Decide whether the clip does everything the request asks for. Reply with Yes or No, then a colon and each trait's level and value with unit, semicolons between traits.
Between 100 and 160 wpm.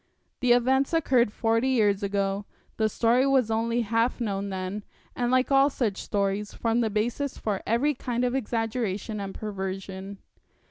Yes: average, 155 wpm